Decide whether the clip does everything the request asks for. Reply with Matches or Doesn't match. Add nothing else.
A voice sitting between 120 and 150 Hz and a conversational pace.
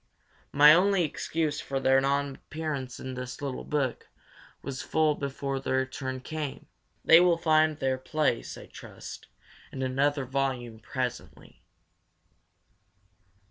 Doesn't match